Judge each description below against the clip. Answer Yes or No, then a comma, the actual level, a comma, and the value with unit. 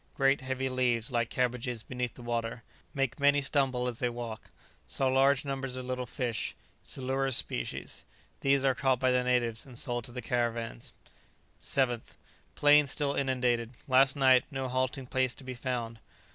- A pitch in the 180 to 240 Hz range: No, low, 130 Hz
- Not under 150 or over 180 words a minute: Yes, average, 165 wpm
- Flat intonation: Yes, narrow, 1.8 semitones